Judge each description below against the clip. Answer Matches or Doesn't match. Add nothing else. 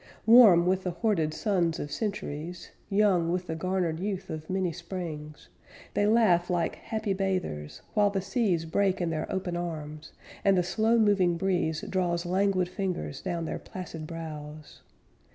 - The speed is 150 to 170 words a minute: Matches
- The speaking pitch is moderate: Matches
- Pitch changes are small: Doesn't match